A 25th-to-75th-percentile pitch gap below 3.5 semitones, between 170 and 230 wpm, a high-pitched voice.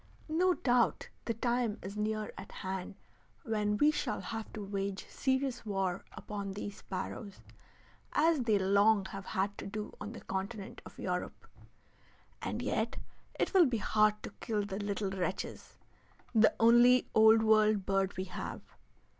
No: average, 2.7 semitones; average, 155 wpm; high, 210 Hz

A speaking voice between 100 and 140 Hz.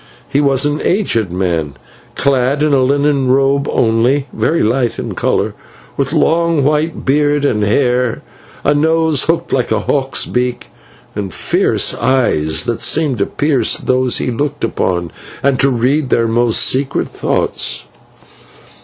Yes: low, 135 Hz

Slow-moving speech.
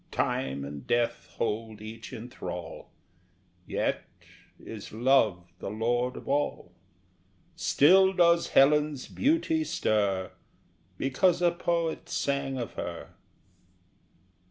Yes: slow, 105 wpm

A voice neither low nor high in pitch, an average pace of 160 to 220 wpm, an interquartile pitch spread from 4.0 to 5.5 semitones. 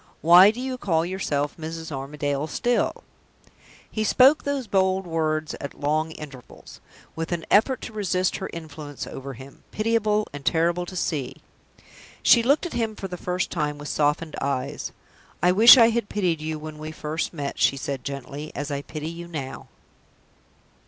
Yes: medium, 165 Hz; average, 170 wpm; average, 5.1 semitones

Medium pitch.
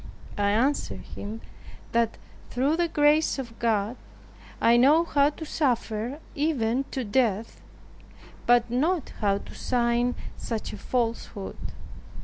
No: high, 245 Hz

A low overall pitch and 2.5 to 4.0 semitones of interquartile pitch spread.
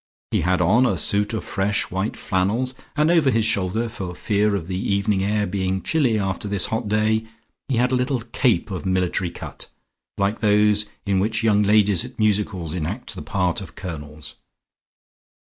Yes: low, 105 Hz; average, 2.9 semitones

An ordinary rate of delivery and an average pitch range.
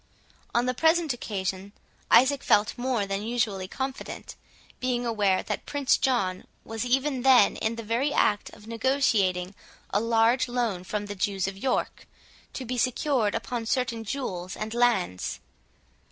Yes: average, 150 wpm; average, 3.9 semitones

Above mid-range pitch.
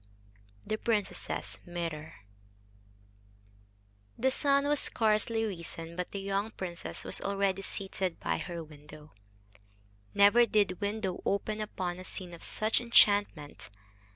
Yes: high, 195 Hz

